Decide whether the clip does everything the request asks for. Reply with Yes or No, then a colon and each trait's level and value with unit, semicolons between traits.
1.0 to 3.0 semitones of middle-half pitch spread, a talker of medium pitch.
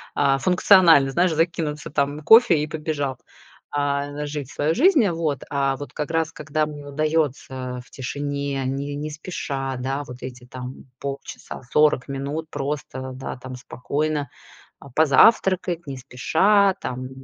Yes: narrow, 2.6 semitones; medium, 145 Hz